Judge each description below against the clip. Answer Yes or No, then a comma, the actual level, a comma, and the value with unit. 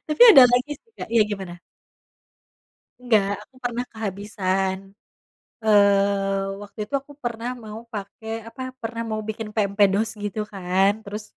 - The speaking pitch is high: Yes, high, 210 Hz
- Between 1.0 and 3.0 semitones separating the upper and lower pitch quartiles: Yes, narrow, 2.5 semitones